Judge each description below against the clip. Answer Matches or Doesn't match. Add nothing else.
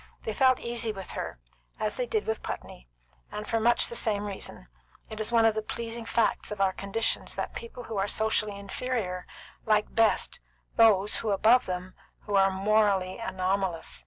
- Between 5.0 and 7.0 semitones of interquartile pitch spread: Doesn't match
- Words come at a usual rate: Matches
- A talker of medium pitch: Doesn't match